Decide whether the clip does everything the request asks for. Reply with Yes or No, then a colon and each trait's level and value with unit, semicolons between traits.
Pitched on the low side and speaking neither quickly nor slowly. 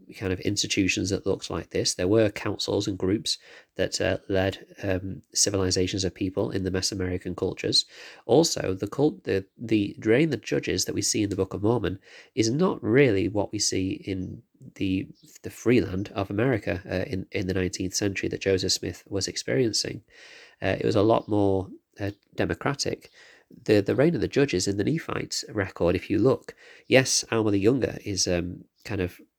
Yes: low, 100 Hz; average, 190 wpm